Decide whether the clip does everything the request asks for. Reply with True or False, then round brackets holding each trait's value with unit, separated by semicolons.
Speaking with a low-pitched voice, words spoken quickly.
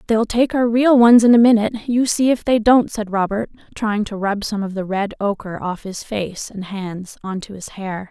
False (215 Hz; 235 wpm)